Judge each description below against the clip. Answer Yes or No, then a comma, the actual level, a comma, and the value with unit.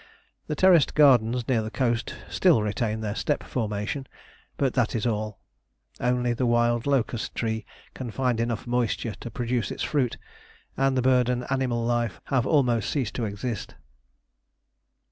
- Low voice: Yes, low, 120 Hz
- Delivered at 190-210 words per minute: No, average, 150 wpm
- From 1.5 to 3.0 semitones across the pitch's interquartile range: Yes, narrow, 2.5 semitones